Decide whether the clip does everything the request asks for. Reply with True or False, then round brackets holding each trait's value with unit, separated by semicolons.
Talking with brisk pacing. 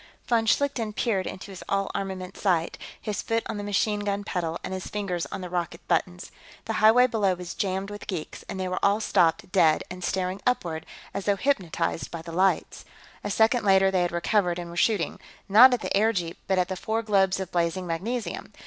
True (210 wpm)